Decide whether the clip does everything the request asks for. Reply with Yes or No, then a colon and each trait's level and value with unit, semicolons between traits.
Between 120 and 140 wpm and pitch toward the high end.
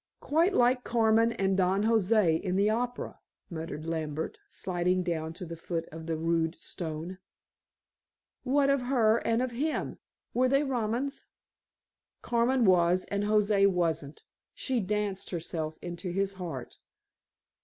Yes: slow, 135 wpm; high, 195 Hz